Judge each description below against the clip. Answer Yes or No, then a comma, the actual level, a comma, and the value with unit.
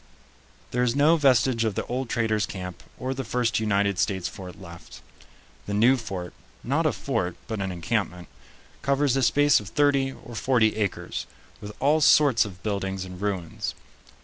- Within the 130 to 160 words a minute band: No, average, 170 wpm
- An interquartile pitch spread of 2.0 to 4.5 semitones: No, average, 5.3 semitones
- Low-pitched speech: Yes, low, 110 Hz